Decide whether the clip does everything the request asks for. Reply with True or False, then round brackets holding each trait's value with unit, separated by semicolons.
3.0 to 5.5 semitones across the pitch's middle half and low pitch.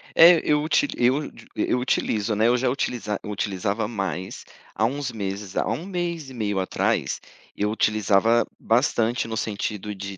True (4.1 semitones; 110 Hz)